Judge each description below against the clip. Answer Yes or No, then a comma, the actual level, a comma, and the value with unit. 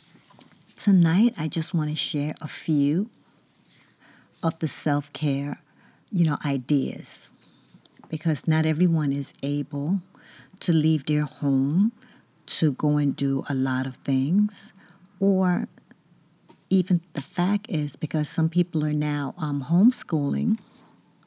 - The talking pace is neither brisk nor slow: No, slow, 120 wpm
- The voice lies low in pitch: No, medium, 155 Hz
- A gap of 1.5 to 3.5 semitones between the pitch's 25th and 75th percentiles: No, average, 4.1 semitones